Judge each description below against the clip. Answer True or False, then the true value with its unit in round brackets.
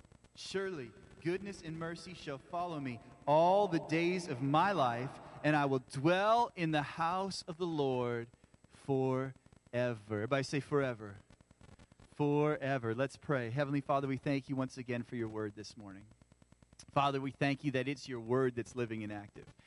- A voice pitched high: False (135 Hz)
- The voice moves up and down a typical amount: True (4.2 semitones)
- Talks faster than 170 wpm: False (165 wpm)